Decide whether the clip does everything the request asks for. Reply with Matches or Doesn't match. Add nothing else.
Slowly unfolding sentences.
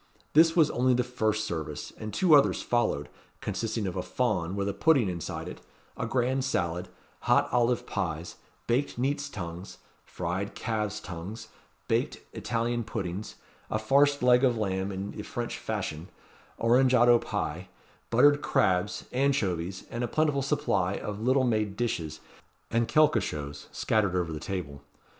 Doesn't match